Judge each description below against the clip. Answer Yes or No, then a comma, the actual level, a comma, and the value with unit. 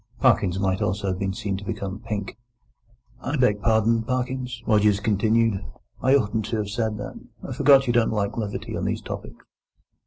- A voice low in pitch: Yes, low, 110 Hz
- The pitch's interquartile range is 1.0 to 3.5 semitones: Yes, average, 2.8 semitones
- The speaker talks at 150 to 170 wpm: No, average, 180 wpm